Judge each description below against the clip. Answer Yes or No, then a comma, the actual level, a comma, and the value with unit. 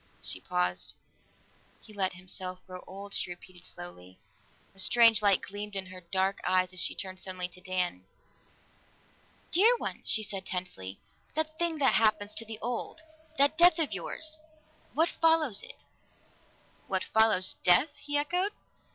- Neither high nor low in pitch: No, high, 200 Hz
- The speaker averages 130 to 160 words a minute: Yes, average, 150 wpm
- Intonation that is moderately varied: No, wide, 7.7 semitones